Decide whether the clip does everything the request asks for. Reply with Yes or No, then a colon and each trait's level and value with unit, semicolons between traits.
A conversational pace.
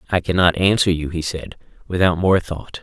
Yes: average, 190 wpm